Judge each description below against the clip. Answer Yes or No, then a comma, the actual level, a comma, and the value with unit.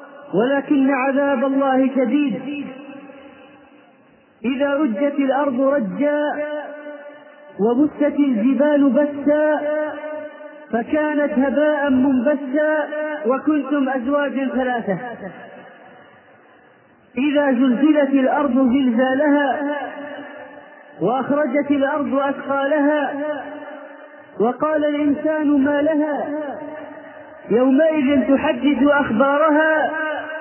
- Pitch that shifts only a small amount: Yes, narrow, 1.5 semitones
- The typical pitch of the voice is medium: No, very high, 285 Hz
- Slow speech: Yes, slow, 60 wpm